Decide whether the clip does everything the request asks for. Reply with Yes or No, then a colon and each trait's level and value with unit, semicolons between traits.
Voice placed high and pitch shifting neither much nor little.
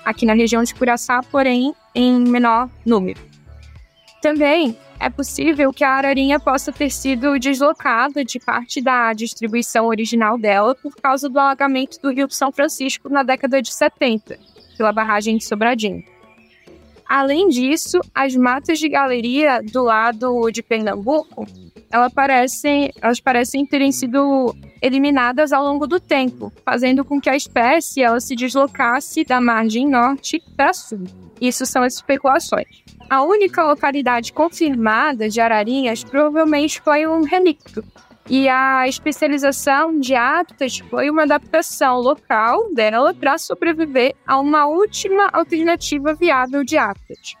Yes: very high, 270 Hz; average, 3.6 semitones